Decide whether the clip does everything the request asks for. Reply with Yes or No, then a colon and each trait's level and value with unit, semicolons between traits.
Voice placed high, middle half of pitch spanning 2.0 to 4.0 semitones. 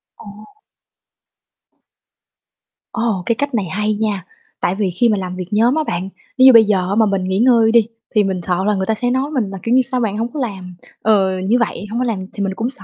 Yes: high, 215 Hz; average, 3.7 semitones